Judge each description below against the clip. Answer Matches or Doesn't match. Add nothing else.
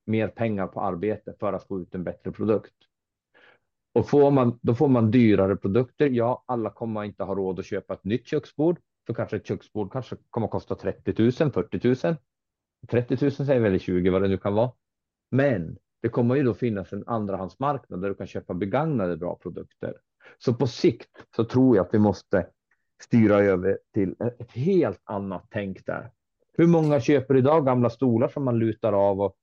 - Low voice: Matches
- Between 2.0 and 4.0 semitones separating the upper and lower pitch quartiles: Doesn't match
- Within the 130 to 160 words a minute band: Doesn't match